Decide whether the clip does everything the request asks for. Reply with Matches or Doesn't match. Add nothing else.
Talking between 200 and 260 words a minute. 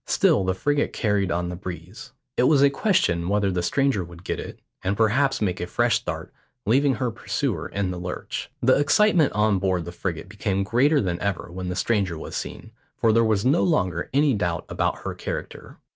Matches